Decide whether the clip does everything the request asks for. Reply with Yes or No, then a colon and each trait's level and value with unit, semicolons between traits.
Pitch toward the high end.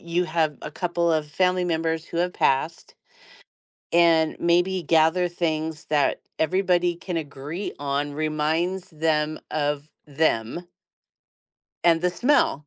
No: medium, 160 Hz